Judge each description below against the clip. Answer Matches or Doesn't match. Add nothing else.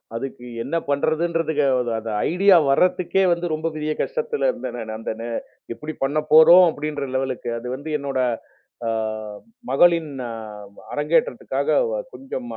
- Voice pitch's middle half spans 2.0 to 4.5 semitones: Matches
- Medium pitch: Matches